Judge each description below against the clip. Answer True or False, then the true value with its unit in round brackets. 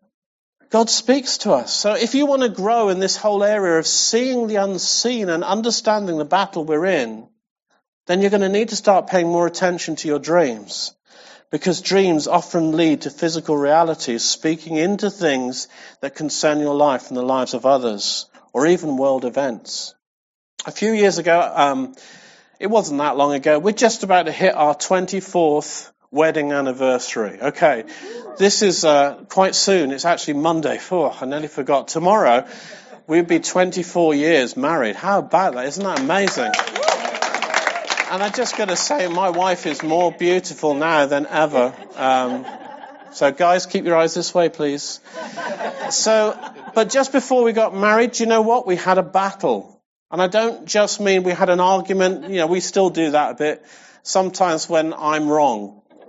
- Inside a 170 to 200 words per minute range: True (175 wpm)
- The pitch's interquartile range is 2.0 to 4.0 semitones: False (5.3 semitones)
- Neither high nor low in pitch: True (180 Hz)